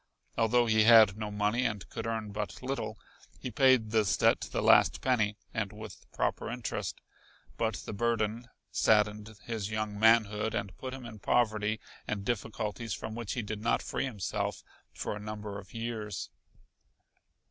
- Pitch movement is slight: Yes, narrow, 1.9 semitones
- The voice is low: Yes, low, 110 Hz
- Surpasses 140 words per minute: Yes, average, 165 wpm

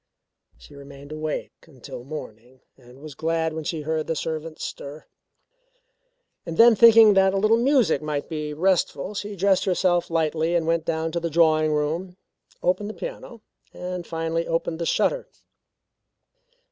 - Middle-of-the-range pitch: Yes, medium, 165 Hz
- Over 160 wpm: No, average, 150 wpm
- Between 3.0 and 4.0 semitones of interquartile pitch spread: Yes, average, 3.3 semitones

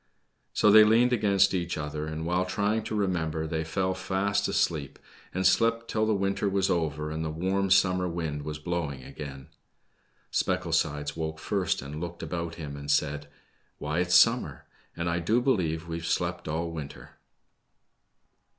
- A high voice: No, very low, 85 Hz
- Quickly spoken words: No, average, 165 wpm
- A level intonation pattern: No, average, 4.1 semitones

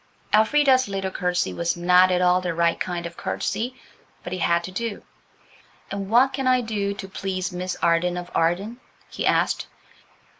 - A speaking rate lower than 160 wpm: No, average, 175 wpm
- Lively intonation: No, average, 3.5 semitones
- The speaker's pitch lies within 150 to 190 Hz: Yes, medium, 185 Hz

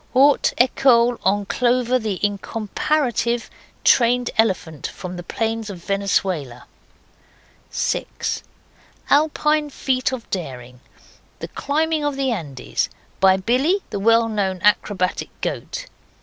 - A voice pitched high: Yes, high, 225 Hz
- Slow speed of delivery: Yes, slow, 110 wpm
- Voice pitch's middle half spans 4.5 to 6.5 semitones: Yes, average, 5.3 semitones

